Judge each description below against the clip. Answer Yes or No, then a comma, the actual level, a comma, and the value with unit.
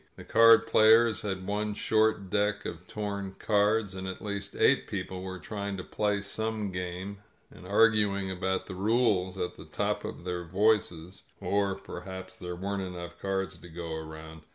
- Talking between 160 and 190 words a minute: Yes, average, 175 wpm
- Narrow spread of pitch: Yes, narrow, 2.3 semitones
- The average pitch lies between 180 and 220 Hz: No, very low, 95 Hz